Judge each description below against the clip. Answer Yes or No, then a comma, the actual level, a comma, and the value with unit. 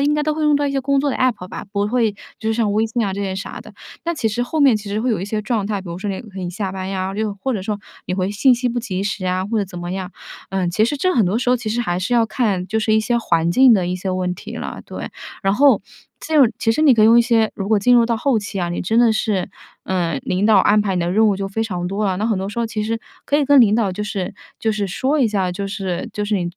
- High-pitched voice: Yes, high, 210 Hz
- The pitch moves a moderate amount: Yes, average, 3.8 semitones